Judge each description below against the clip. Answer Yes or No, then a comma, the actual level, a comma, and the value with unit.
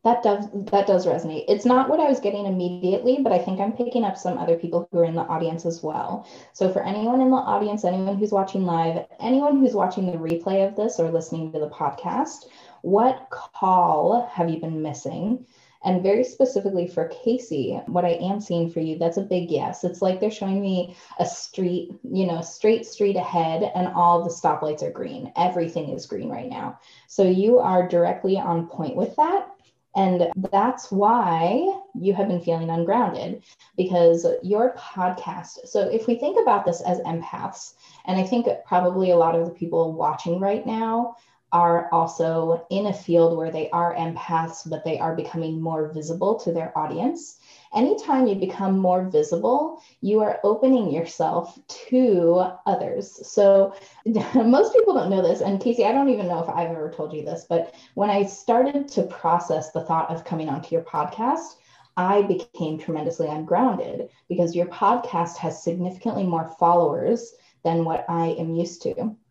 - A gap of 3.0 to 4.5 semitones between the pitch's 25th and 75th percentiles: No, average, 5.0 semitones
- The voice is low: No, medium, 185 Hz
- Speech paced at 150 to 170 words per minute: No, average, 180 wpm